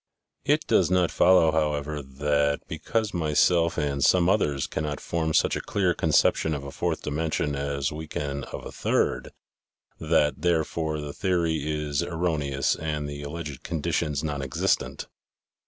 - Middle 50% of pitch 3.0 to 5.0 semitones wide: No, narrow, 2.5 semitones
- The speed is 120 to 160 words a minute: Yes, average, 150 wpm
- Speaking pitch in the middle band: No, very low, 75 Hz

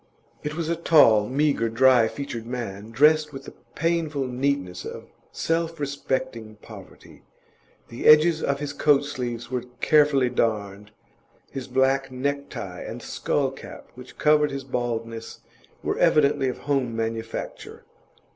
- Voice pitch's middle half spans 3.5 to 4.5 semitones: Yes, average, 4.1 semitones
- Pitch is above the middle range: No, low, 135 Hz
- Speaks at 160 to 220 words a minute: No, slow, 135 wpm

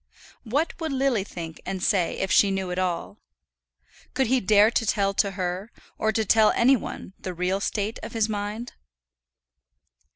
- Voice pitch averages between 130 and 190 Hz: No, high, 205 Hz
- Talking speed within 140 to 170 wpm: Yes, average, 165 wpm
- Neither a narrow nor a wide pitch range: Yes, average, 3.1 semitones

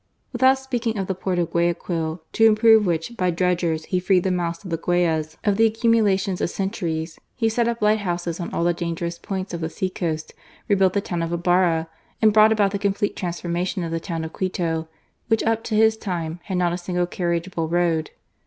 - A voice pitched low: No, medium, 180 Hz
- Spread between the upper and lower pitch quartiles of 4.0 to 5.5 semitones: No, average, 3.5 semitones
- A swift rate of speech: Yes, fast, 210 wpm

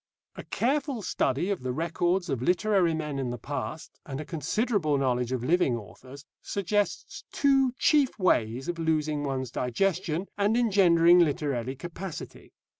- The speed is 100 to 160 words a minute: Yes, average, 145 wpm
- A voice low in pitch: No, medium, 160 Hz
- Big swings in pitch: Yes, wide, 6.4 semitones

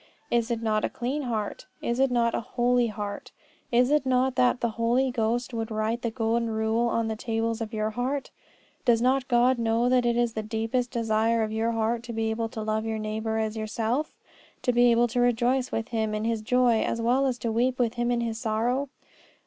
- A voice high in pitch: Yes, high, 230 Hz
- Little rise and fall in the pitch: Yes, narrow, 1.8 semitones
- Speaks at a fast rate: Yes, fast, 220 wpm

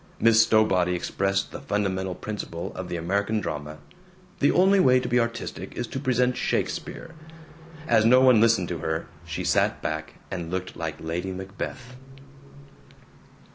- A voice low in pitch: Yes, low, 100 Hz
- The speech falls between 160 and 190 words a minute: No, average, 150 wpm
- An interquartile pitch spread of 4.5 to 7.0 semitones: Yes, wide, 5.4 semitones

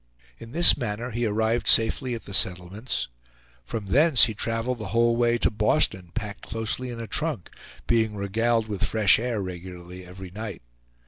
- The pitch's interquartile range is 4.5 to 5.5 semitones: No, average, 3.0 semitones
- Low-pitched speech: Yes, low, 110 Hz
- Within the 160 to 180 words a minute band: Yes, average, 170 wpm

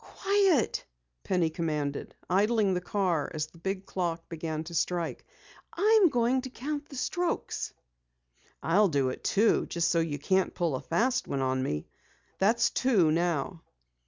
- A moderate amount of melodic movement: No, wide, 6.7 semitones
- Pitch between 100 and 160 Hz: No, medium, 180 Hz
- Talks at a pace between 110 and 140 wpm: No, average, 155 wpm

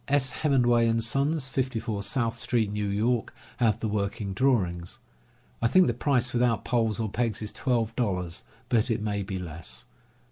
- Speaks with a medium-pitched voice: No, low, 115 Hz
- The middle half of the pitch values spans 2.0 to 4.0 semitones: Yes, average, 3.4 semitones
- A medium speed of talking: Yes, average, 175 wpm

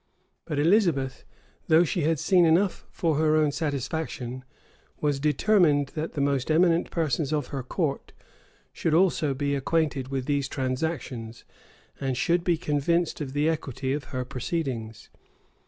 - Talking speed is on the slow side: No, average, 150 wpm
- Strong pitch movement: No, average, 3.4 semitones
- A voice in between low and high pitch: Yes, medium, 145 Hz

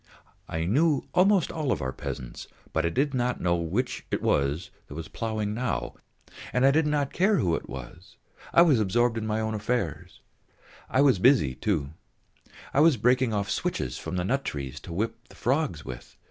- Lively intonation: Yes, wide, 8.2 semitones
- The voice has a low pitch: Yes, low, 110 Hz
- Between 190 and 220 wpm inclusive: No, average, 180 wpm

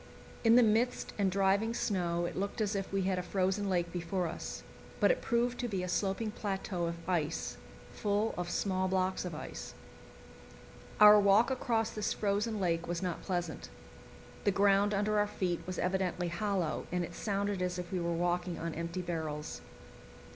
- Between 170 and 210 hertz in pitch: Yes, high, 190 Hz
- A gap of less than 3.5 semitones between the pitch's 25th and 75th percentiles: Yes, average, 2.8 semitones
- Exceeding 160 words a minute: Yes, average, 180 wpm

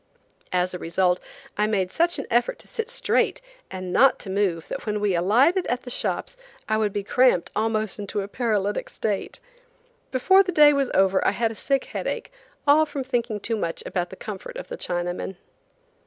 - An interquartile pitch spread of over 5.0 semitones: Yes, wide, 5.4 semitones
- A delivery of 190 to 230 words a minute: Yes, average, 195 wpm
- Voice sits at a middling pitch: No, high, 215 Hz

